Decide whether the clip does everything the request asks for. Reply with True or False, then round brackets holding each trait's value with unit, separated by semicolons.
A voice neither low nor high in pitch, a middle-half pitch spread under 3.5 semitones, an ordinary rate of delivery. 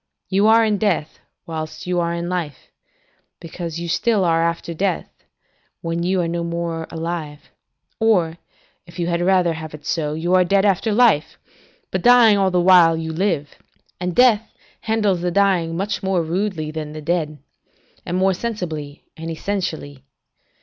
True (175 Hz; 2.9 semitones; 165 wpm)